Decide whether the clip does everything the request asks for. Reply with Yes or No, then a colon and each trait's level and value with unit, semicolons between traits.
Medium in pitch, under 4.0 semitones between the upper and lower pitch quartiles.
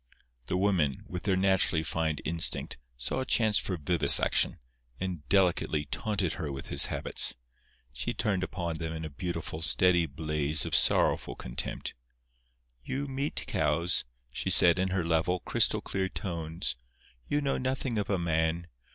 No: very low, 85 Hz; average, 3.3 semitones